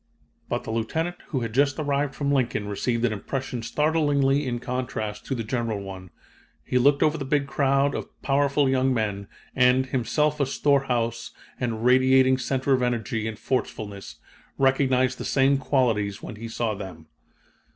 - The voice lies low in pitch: Yes, low, 130 Hz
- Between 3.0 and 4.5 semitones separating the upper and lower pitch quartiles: Yes, average, 3.3 semitones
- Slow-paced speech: No, average, 160 wpm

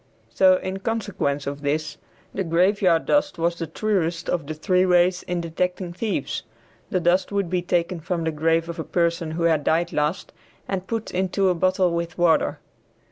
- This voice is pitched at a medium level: Yes, medium, 175 Hz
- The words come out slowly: No, average, 185 wpm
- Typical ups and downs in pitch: No, narrow, 2.3 semitones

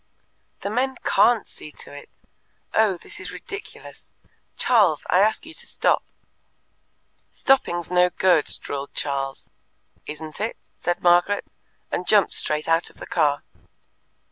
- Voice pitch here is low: No, medium, 180 Hz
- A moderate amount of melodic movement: No, wide, 5.8 semitones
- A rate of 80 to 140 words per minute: Yes, slow, 135 wpm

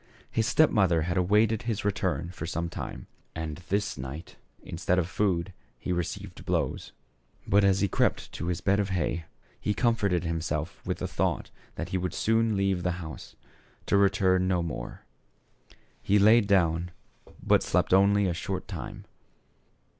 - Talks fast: No, average, 160 wpm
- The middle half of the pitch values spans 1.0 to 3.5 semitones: Yes, average, 3.0 semitones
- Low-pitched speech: Yes, very low, 95 Hz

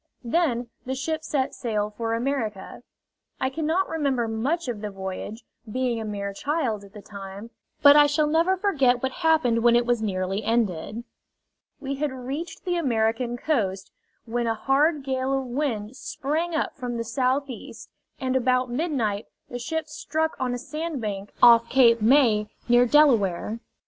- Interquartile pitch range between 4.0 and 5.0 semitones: Yes, average, 4.6 semitones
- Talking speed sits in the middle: Yes, average, 160 wpm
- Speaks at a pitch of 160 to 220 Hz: No, very high, 250 Hz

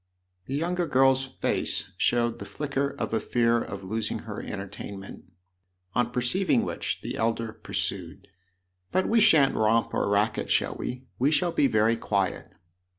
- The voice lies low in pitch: Yes, low, 115 Hz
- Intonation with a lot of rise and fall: No, average, 4.1 semitones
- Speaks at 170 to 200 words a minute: No, average, 155 wpm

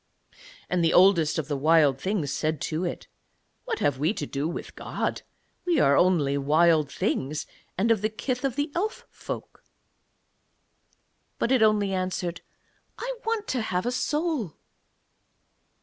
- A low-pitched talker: No, medium, 185 Hz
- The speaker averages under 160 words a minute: Yes, average, 150 wpm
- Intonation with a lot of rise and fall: Yes, wide, 8.1 semitones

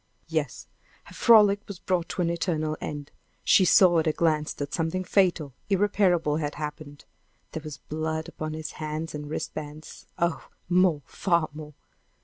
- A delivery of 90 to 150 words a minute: No, average, 160 wpm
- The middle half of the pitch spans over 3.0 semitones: No, average, 2.7 semitones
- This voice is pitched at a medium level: Yes, medium, 160 Hz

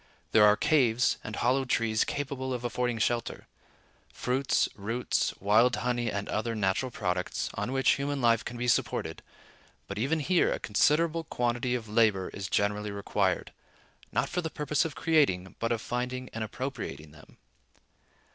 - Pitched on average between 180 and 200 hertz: No, low, 120 Hz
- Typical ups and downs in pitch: Yes, average, 3.8 semitones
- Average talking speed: Yes, average, 155 wpm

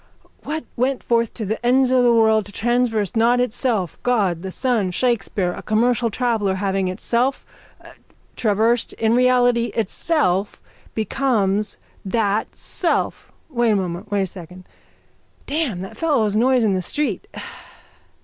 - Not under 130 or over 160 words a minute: Yes, average, 140 wpm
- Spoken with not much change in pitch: No, average, 3.8 semitones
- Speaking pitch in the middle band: No, high, 225 Hz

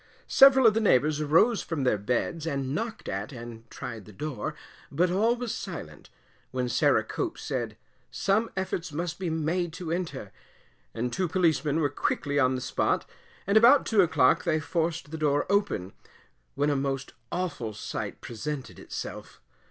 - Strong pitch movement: Yes, wide, 5.9 semitones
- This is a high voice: No, medium, 155 Hz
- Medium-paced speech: Yes, average, 165 wpm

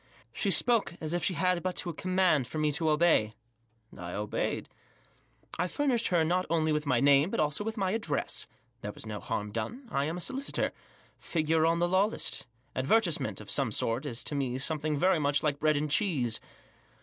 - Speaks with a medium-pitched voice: Yes, medium, 155 Hz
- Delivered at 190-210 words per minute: Yes, average, 200 wpm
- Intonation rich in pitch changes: No, average, 4.6 semitones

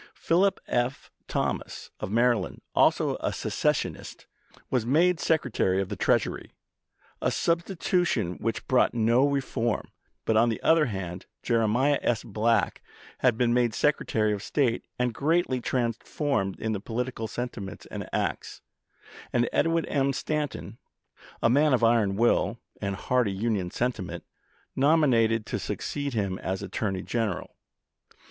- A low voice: Yes, low, 120 Hz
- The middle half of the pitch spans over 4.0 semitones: Yes, average, 4.4 semitones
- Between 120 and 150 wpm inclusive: Yes, average, 140 wpm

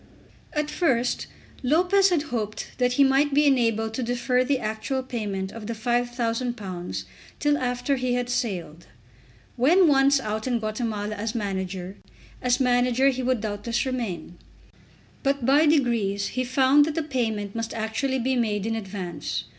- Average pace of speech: Yes, average, 155 wpm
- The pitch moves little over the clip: No, average, 3.6 semitones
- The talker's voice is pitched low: No, high, 245 Hz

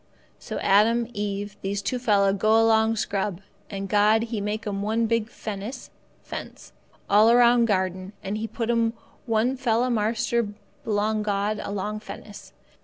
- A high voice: Yes, high, 215 Hz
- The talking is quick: No, average, 150 wpm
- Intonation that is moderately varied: No, narrow, 2.1 semitones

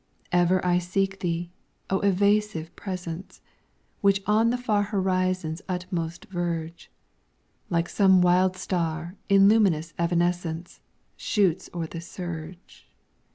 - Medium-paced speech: No, slow, 110 wpm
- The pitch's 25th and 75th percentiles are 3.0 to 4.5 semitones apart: No, narrow, 2.5 semitones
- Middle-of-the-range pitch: Yes, medium, 180 Hz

